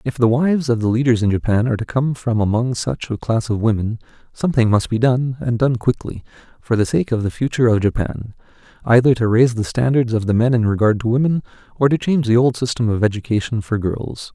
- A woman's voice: No, male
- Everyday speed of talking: No, fast, 230 wpm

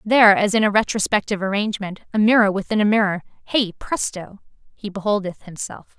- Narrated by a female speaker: Yes, female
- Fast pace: No, average, 160 wpm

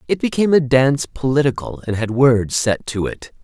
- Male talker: Yes, male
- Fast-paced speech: No, average, 190 wpm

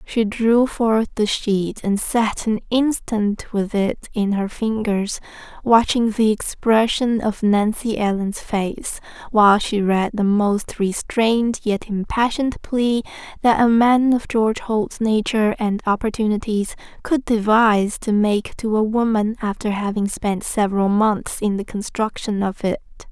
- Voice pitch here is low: No, high, 215 Hz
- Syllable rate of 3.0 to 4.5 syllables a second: Yes, 4.1 syllables/s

